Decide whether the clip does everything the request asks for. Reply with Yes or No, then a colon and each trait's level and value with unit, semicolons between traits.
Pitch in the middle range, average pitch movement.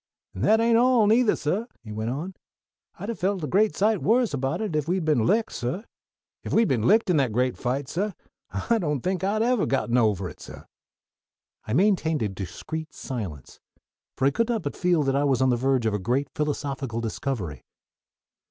No: medium, 150 Hz; wide, 8.8 semitones